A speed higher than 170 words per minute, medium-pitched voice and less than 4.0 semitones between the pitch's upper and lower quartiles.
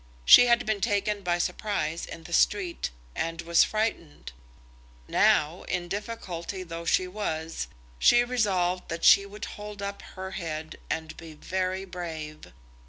No: average, 145 wpm; medium, 180 Hz; average, 3.6 semitones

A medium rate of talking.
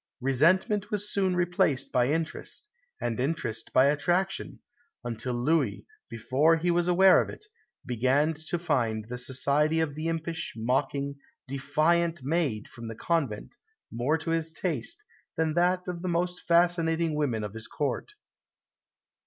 Yes: average, 145 wpm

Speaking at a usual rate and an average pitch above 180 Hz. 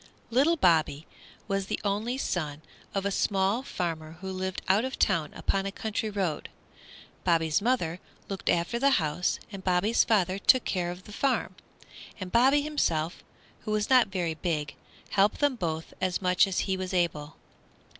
Yes: average, 165 wpm; high, 190 Hz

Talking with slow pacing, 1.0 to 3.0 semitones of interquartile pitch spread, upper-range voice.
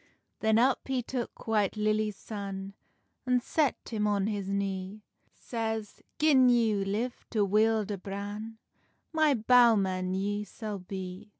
Yes: slow, 130 wpm; narrow, 2.6 semitones; high, 215 Hz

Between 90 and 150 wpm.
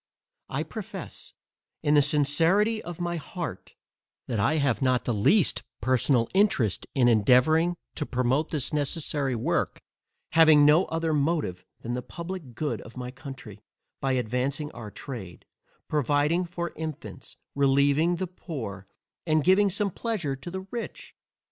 Yes: average, 140 wpm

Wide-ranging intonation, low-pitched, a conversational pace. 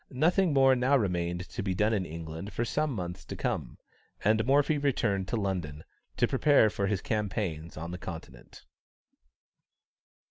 Yes: wide, 6.9 semitones; low, 100 Hz; average, 155 wpm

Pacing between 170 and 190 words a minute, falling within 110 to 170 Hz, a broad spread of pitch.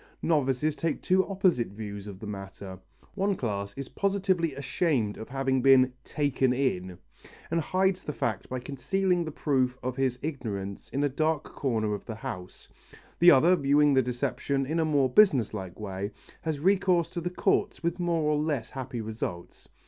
Yes: average, 175 wpm; low, 135 Hz; wide, 6.6 semitones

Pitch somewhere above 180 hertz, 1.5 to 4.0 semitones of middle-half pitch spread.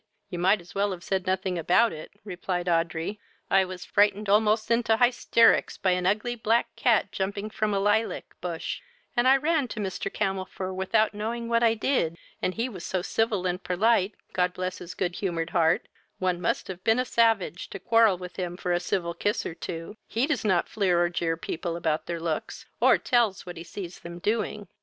Yes: high, 190 Hz; average, 3.7 semitones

